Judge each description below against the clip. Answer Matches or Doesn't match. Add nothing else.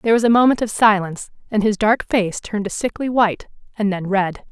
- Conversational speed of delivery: Doesn't match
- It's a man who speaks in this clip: Doesn't match